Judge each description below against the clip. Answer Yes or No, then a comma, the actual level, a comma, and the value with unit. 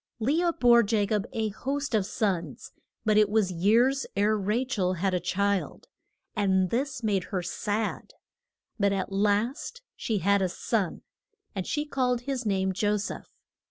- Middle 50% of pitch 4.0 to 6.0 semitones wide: No, average, 3.5 semitones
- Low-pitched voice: No, high, 210 Hz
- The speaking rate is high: No, average, 165 wpm